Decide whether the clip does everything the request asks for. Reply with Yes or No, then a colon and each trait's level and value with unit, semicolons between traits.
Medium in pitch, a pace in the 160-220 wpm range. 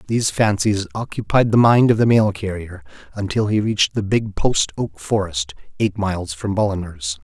No: low, 100 Hz; average, 170 wpm